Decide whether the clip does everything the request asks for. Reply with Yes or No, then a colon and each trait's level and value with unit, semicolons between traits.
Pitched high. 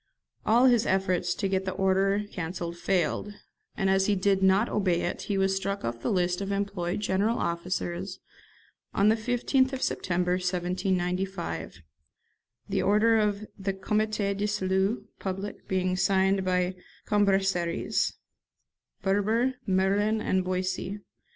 Yes: high, 195 Hz